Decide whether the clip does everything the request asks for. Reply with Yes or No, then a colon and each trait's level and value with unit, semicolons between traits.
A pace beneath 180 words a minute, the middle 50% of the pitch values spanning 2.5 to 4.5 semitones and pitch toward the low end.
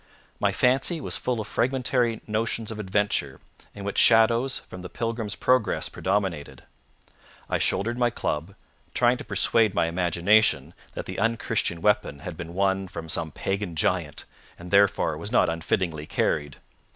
No: average, 150 wpm; average, 5.2 semitones; low, 100 Hz